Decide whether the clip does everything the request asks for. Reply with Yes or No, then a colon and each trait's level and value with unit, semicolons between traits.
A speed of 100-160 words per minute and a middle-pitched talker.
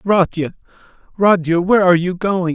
Yes: average, 140 wpm; medium, 180 Hz